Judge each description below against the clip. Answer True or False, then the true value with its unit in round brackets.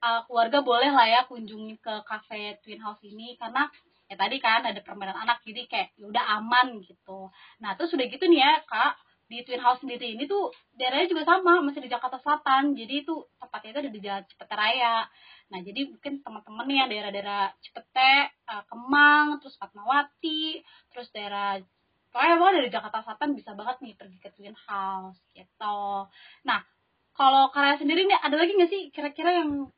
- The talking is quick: True (175 wpm)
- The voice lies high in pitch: True (245 Hz)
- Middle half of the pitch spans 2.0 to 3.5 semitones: False (5.6 semitones)